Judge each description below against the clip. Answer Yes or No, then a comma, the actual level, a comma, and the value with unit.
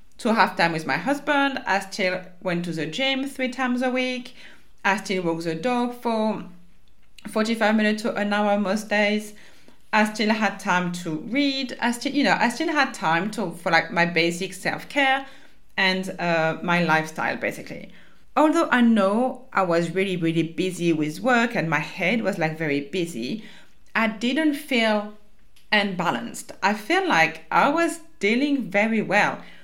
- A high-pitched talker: Yes, high, 205 Hz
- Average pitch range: No, wide, 6.2 semitones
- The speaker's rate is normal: Yes, average, 170 wpm